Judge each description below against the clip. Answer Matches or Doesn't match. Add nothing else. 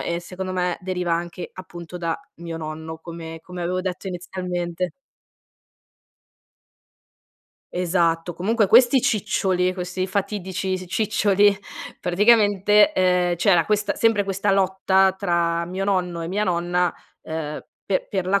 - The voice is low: Doesn't match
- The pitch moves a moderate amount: Doesn't match